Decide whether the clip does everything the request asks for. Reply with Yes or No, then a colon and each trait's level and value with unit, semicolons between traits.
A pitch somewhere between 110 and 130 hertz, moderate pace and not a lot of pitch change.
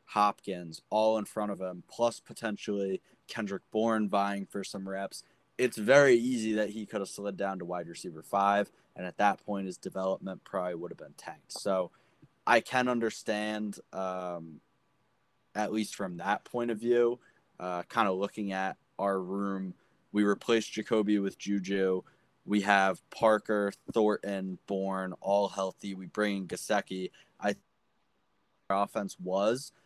No: low, 100 Hz; average, 155 wpm; narrow, 2.3 semitones